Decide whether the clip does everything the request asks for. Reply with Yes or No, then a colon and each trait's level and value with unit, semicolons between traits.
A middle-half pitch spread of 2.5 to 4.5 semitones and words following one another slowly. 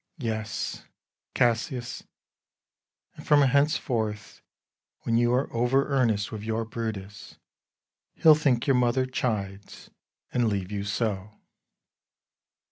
Yes: average, 3.4 semitones; slow, 110 wpm